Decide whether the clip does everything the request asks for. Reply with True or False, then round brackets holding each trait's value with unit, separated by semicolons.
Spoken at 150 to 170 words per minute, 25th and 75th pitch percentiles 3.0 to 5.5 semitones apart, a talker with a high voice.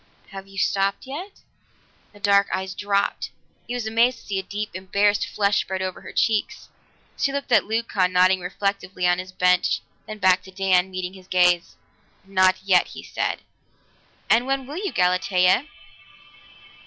False (165 wpm; 2.5 semitones; 195 Hz)